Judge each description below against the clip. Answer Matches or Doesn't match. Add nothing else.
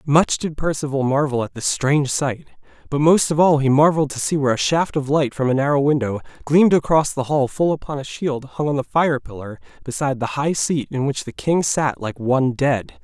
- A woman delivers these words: Doesn't match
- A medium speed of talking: Doesn't match